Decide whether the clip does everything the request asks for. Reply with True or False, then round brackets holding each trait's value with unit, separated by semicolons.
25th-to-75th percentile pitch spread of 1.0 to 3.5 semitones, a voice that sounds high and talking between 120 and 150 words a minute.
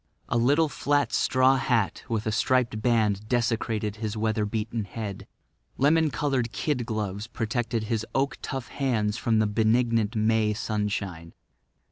False (2.8 semitones; 115 Hz; 140 wpm)